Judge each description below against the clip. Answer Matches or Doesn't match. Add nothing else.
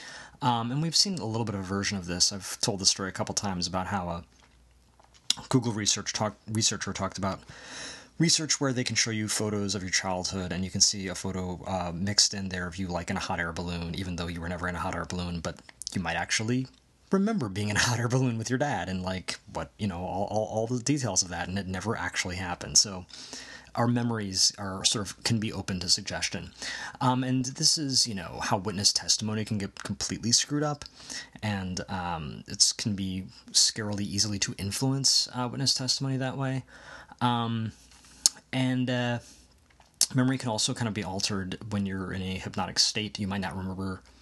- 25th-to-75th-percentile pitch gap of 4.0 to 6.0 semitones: Matches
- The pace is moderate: Doesn't match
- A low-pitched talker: Matches